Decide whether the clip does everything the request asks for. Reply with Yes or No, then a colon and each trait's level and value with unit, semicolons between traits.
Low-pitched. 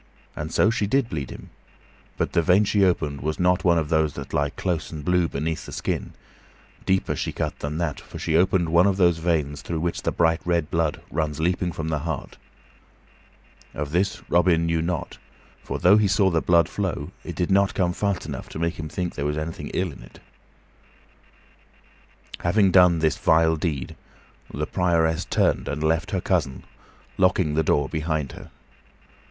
Yes: very low, 85 Hz